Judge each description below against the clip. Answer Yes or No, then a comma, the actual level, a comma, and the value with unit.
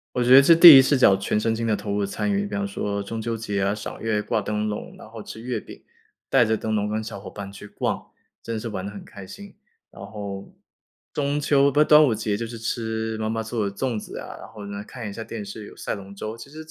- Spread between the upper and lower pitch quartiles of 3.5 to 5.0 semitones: No, average, 3.1 semitones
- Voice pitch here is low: Yes, low, 110 Hz